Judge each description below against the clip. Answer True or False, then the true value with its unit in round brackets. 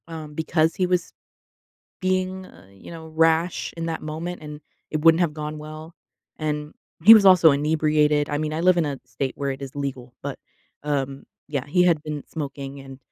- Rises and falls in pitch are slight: True (2.3 semitones)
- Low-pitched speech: False (155 Hz)